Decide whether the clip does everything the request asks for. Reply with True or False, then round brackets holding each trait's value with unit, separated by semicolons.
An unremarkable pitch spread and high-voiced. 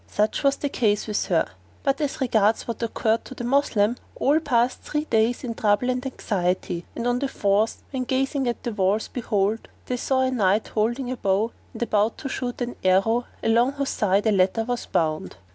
True (3.7 semitones; 235 Hz)